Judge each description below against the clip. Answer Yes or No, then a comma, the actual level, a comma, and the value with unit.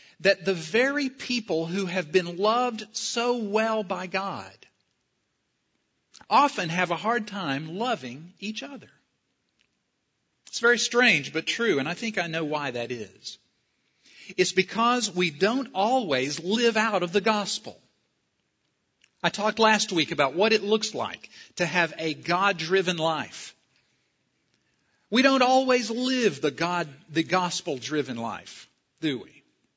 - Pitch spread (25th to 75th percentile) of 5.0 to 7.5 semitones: Yes, wide, 5.4 semitones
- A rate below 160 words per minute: Yes, slow, 135 wpm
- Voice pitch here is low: No, high, 195 Hz